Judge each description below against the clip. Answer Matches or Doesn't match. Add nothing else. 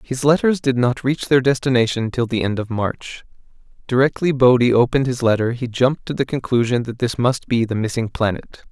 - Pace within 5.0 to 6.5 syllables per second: Matches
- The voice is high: Doesn't match